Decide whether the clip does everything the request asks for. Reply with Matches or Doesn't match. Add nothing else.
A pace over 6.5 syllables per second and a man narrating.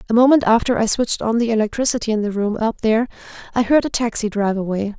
Doesn't match